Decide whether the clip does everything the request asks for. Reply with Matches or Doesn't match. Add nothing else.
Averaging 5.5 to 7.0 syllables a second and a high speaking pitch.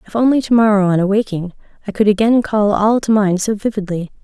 Matches